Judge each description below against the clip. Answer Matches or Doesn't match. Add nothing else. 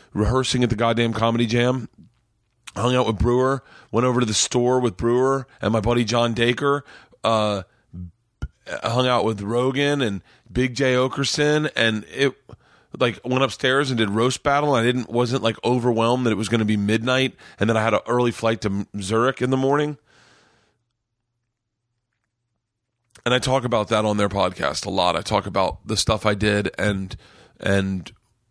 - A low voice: Matches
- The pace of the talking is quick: Doesn't match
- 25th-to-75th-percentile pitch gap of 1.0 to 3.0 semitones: Matches